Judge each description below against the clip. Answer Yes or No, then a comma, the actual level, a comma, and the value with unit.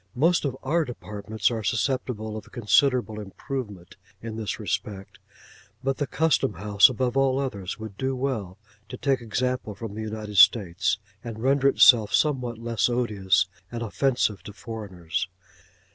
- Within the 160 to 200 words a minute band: No, average, 145 wpm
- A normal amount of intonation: Yes, average, 4.0 semitones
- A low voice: Yes, low, 115 Hz